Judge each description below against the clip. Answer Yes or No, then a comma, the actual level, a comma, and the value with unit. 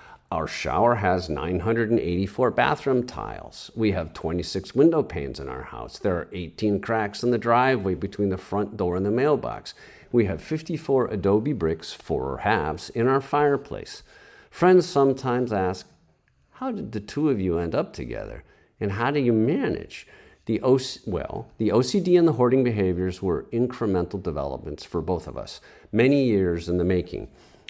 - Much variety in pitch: Yes, wide, 5.9 semitones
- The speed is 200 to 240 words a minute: No, average, 165 wpm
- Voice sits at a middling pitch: No, low, 110 Hz